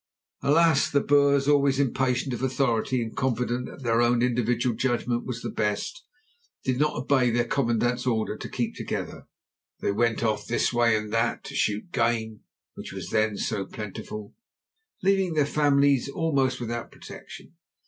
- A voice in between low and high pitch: No, low, 125 Hz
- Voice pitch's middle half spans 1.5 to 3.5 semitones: Yes, average, 3.2 semitones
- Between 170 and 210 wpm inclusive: No, average, 160 wpm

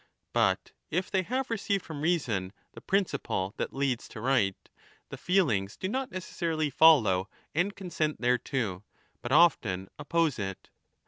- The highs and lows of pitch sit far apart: Yes, wide, 8.8 semitones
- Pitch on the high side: No, medium, 145 Hz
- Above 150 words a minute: No, average, 140 wpm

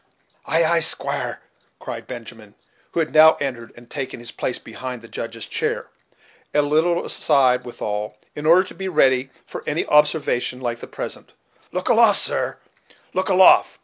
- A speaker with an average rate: Yes, average, 160 wpm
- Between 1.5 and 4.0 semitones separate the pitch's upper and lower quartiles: No, average, 5.1 semitones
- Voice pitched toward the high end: No, low, 135 Hz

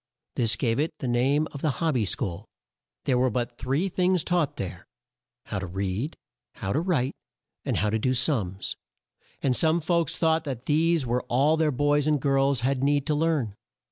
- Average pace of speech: Yes, average, 190 wpm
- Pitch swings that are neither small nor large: Yes, average, 4.5 semitones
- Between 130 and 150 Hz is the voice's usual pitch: Yes, medium, 140 Hz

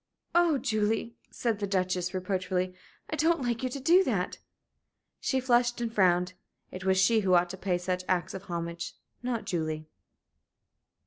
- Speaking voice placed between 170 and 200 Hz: Yes, high, 190 Hz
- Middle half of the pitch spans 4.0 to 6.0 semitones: Yes, average, 4.8 semitones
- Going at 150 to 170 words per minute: Yes, average, 165 wpm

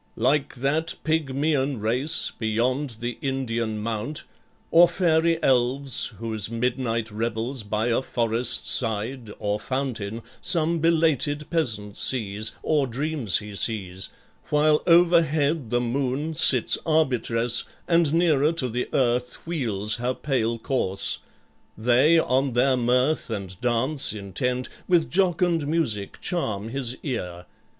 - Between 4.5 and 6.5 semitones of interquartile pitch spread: Yes, average, 5.0 semitones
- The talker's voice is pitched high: No, low, 125 Hz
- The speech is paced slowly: Yes, slow, 120 wpm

